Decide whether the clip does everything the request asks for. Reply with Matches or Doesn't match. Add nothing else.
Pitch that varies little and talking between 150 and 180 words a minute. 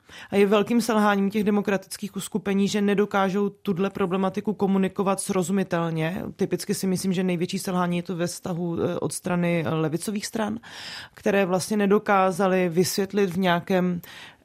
Doesn't match